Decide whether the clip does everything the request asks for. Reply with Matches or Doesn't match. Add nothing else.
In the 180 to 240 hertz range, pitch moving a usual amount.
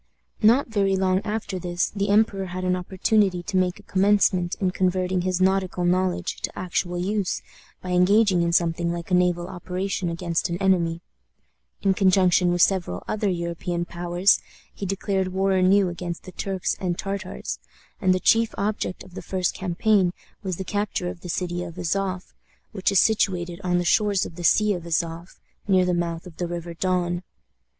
Doesn't match